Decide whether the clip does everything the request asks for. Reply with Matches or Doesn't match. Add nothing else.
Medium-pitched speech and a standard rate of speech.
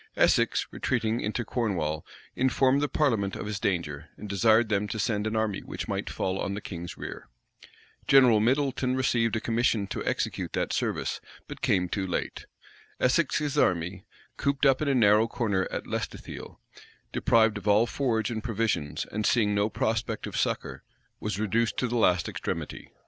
Doesn't match